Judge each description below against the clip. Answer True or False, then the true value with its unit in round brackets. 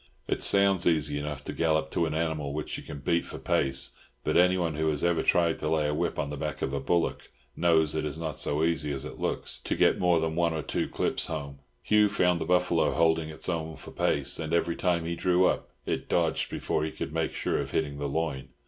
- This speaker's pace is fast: True (245 wpm)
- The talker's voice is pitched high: False (80 Hz)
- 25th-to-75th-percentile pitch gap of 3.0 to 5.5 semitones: False (2.4 semitones)